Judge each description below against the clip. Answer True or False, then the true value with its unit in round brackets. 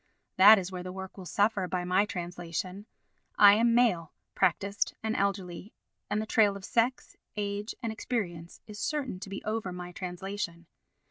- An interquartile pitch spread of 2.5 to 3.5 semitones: True (3.0 semitones)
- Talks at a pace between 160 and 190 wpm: True (165 wpm)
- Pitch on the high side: True (200 Hz)